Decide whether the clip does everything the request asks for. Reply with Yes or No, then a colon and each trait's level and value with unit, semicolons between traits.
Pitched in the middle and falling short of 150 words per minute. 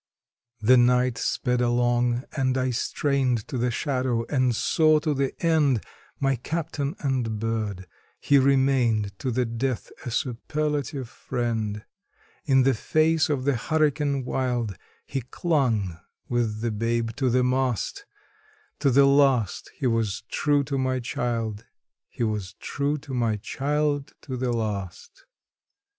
No: low, 125 Hz; average, 140 wpm